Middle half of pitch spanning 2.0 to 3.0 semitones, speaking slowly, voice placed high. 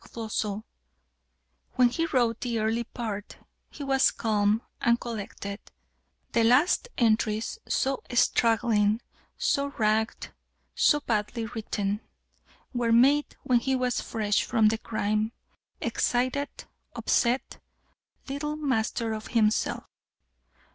Yes: average, 2.7 semitones; slow, 110 wpm; high, 230 Hz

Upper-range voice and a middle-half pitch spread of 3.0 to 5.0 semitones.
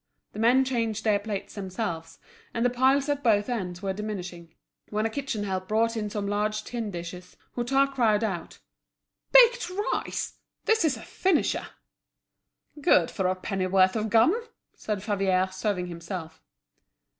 Yes: high, 210 Hz; average, 4.4 semitones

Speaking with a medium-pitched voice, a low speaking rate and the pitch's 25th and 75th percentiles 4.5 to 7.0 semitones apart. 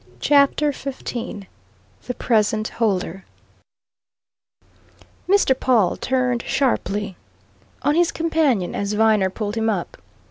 No: high, 220 Hz; slow, 100 wpm; average, 5.1 semitones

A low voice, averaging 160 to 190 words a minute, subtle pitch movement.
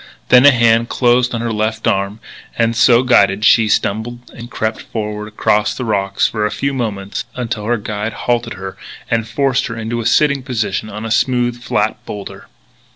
Yes: low, 115 Hz; average, 185 wpm; narrow, 2.3 semitones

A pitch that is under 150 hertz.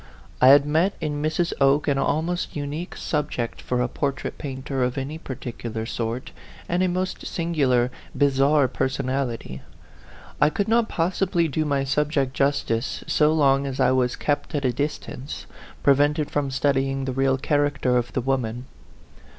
Yes: medium, 140 Hz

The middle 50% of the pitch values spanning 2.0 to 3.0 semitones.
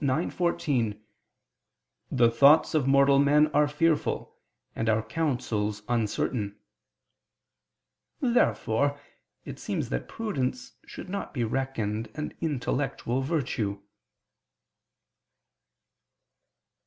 No: average, 5.0 semitones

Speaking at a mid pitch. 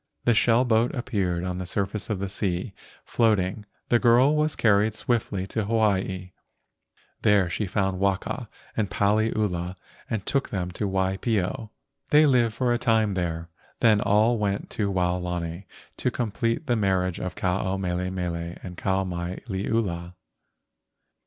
No: low, 100 Hz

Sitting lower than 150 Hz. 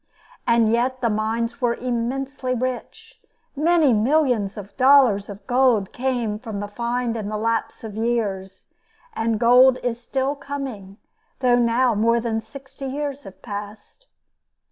No: high, 235 Hz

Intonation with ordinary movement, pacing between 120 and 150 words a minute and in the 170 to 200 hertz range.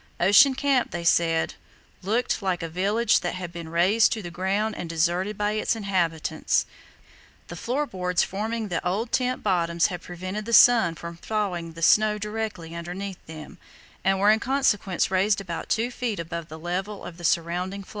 No: average, 3.9 semitones; average, 180 wpm; high, 190 Hz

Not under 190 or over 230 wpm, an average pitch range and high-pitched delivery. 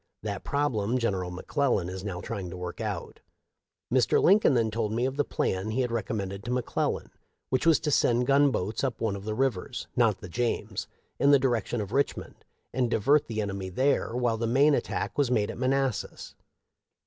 No: fast, 205 wpm; average, 4.7 semitones; low, 115 Hz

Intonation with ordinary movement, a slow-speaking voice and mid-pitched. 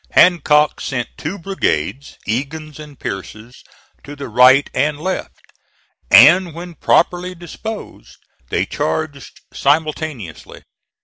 Yes: average, 4.3 semitones; slow, 105 wpm; medium, 150 Hz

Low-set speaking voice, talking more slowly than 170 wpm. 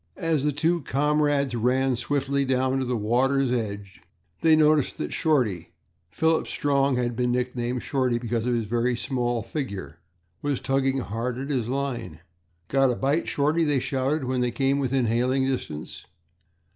Yes: low, 130 Hz; average, 160 wpm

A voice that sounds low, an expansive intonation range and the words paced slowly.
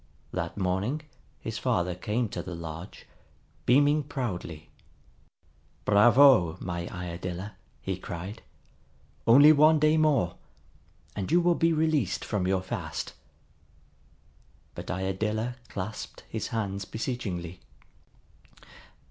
Yes: low, 105 Hz; wide, 7.5 semitones; slow, 105 wpm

